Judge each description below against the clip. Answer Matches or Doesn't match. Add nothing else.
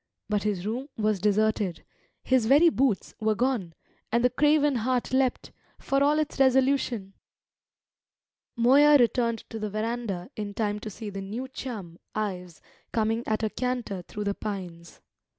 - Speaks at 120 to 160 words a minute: Matches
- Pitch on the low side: Doesn't match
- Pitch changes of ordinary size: Matches